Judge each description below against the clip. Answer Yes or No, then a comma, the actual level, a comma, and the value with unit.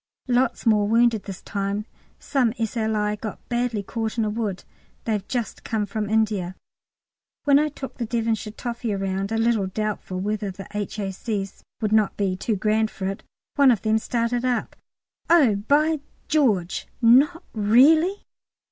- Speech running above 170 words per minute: No, average, 155 wpm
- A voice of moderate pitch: No, high, 220 Hz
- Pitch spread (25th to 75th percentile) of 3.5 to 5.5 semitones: No, average, 2.9 semitones